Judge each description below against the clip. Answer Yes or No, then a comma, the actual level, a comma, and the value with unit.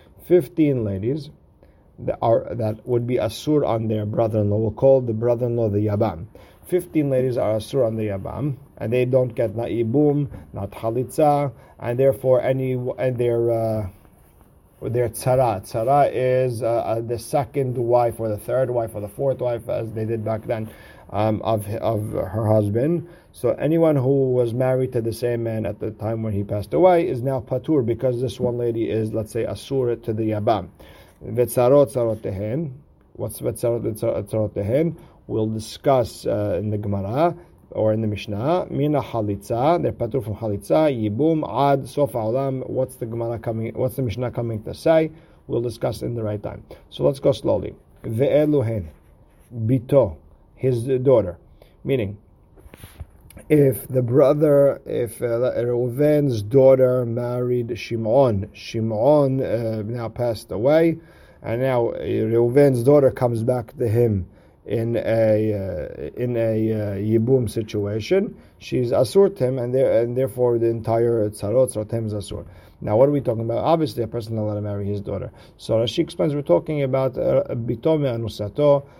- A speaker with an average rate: Yes, average, 155 wpm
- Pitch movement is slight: No, average, 3.5 semitones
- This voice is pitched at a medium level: No, low, 120 Hz